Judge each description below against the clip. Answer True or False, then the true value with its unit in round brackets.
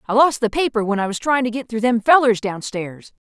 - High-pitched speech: True (230 Hz)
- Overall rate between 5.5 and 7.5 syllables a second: True (5.7 syllables/s)